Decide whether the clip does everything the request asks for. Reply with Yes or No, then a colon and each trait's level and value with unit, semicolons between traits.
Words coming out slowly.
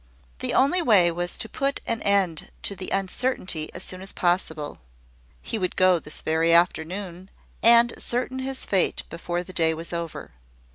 No: average, 165 wpm